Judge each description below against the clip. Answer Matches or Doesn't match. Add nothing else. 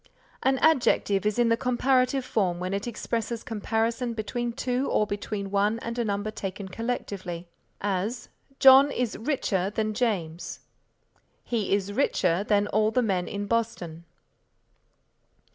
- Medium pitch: Doesn't match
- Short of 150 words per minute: Matches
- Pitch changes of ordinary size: Matches